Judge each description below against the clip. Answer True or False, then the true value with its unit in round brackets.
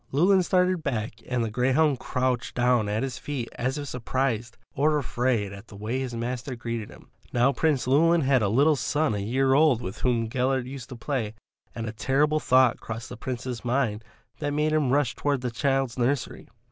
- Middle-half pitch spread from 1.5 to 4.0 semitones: True (3.3 semitones)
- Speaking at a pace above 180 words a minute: True (195 wpm)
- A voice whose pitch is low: True (130 Hz)